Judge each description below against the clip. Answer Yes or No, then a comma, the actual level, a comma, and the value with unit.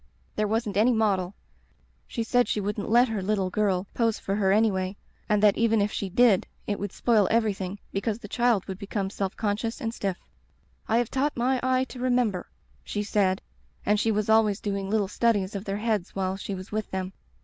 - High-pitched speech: Yes, high, 210 Hz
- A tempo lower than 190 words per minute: No, fast, 205 wpm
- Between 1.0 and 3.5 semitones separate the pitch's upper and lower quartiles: Yes, narrow, 2.6 semitones